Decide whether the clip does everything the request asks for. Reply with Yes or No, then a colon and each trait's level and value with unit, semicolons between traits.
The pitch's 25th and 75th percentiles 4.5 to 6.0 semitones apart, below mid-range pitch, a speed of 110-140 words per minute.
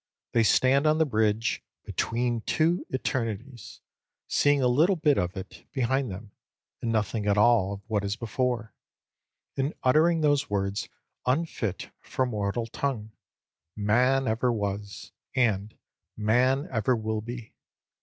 No: average, 4.1 semitones; low, 115 Hz; slow, 135 wpm